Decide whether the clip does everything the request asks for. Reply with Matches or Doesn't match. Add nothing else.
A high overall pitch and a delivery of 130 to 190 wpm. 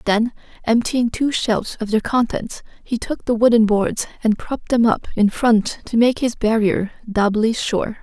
Matches